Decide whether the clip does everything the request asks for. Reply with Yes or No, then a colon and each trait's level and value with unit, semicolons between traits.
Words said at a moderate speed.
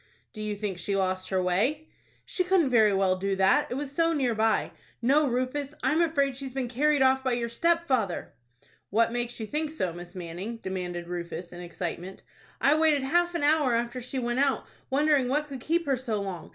No: fast, 210 wpm